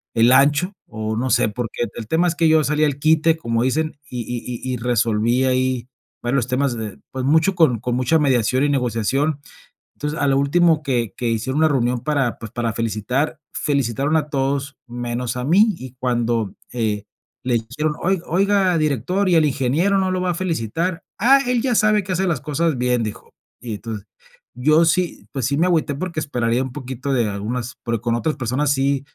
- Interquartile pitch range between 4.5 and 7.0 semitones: Yes, average, 4.8 semitones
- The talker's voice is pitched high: No, low, 135 Hz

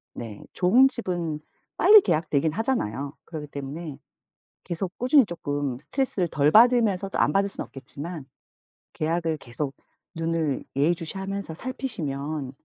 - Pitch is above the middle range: No, medium, 165 Hz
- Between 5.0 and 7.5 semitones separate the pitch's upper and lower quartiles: Yes, wide, 5.4 semitones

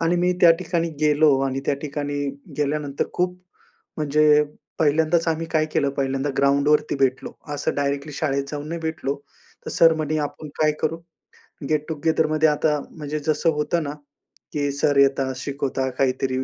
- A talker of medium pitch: Yes, medium, 150 Hz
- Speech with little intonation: Yes, narrow, 2.1 semitones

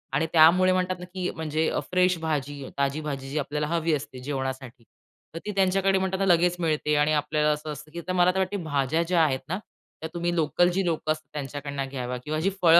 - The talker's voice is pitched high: No, medium, 155 Hz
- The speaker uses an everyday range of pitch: Yes, average, 3.5 semitones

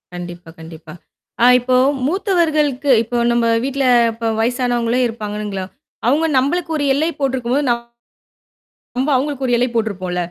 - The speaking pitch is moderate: No, high, 245 Hz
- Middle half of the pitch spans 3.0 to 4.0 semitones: No, average, 4.5 semitones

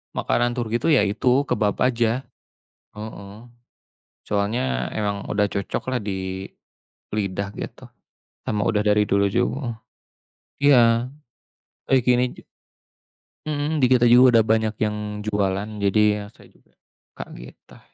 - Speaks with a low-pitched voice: Yes, low, 105 Hz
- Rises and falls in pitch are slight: No, average, 3.2 semitones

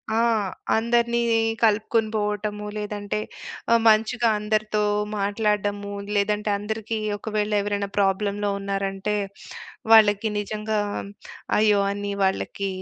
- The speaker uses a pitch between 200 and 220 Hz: Yes, high, 210 Hz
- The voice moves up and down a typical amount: No, narrow, 1.1 semitones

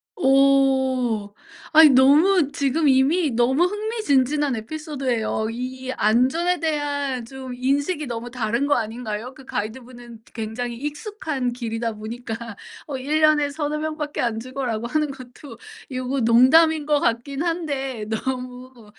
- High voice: Yes, very high, 265 Hz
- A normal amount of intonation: Yes, average, 3.8 semitones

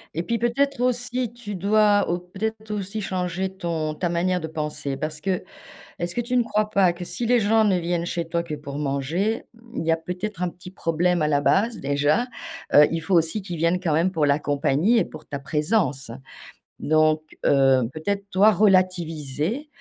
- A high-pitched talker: No, medium, 180 Hz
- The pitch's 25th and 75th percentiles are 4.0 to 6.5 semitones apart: Yes, average, 5.3 semitones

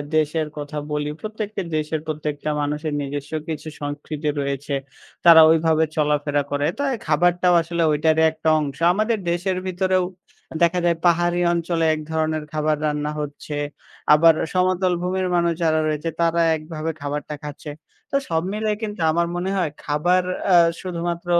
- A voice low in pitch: No, medium, 160 Hz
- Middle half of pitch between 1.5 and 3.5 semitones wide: Yes, average, 2.8 semitones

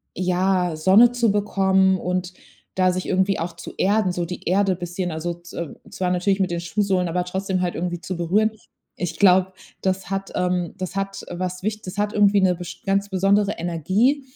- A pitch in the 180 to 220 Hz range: Yes, medium, 185 Hz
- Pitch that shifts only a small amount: Yes, narrow, 1.7 semitones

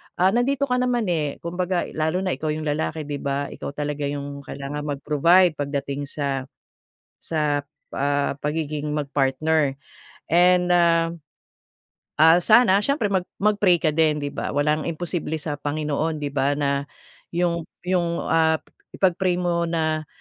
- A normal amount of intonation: Yes, average, 3.4 semitones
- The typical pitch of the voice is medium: Yes, medium, 155 Hz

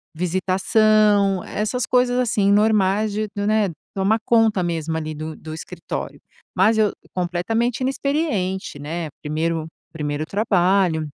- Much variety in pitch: No, average, 4.6 semitones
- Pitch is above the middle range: Yes, high, 195 Hz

